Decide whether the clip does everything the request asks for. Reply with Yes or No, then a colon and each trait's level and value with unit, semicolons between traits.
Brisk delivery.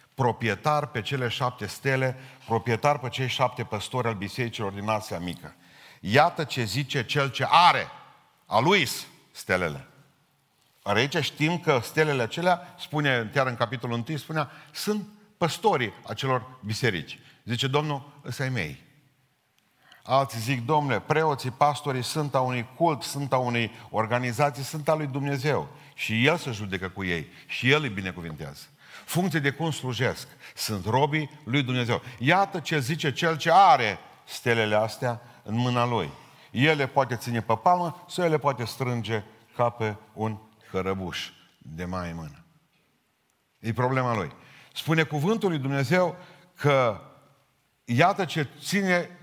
No: average, 145 wpm